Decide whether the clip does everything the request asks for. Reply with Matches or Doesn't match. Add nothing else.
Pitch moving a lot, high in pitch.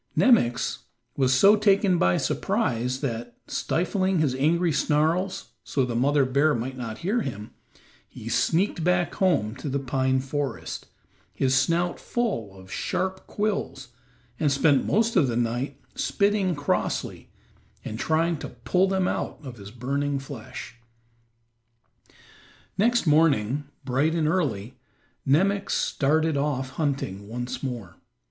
Doesn't match